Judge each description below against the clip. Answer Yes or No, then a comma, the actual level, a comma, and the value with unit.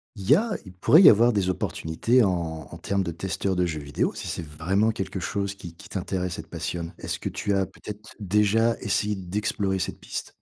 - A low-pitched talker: Yes, very low, 95 Hz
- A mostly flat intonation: No, average, 3.3 semitones